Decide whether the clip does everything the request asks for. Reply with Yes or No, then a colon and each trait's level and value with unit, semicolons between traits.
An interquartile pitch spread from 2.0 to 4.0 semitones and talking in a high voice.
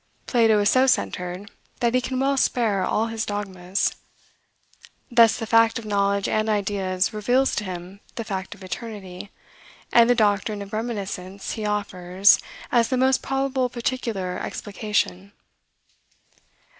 Yes: average, 3.3 semitones; high, 210 Hz